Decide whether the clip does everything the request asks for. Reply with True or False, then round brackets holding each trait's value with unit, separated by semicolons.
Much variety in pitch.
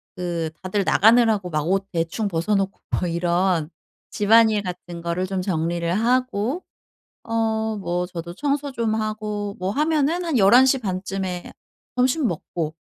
False (4.4 semitones)